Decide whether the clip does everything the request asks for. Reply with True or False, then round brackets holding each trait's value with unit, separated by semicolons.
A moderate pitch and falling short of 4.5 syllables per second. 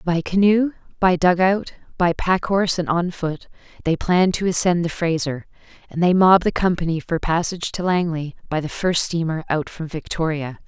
False (175 Hz; 5.2 syllables/s)